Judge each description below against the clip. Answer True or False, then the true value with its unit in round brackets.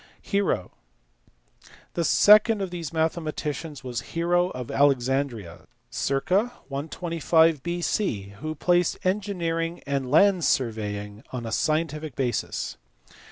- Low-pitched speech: False (155 Hz)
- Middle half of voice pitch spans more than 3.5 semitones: True (5.0 semitones)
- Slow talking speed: True (105 wpm)